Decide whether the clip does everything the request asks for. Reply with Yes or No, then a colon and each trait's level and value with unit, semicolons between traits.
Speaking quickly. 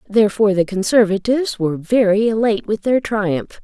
No: average, 150 wpm